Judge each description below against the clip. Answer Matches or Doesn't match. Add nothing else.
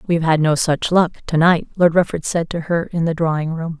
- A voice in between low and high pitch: Matches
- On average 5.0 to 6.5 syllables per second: Matches